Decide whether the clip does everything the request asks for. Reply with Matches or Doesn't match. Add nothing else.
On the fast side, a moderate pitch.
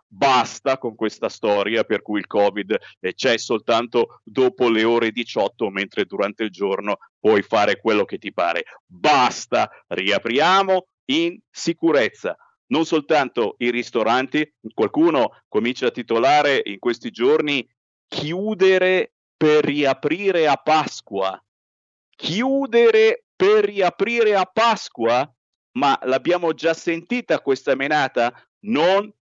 Doesn't match